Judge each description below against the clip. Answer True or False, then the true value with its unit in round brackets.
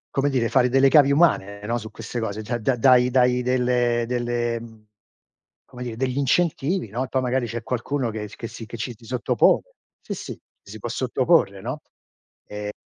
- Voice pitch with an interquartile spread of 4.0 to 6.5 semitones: False (2.4 semitones)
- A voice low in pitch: True (120 Hz)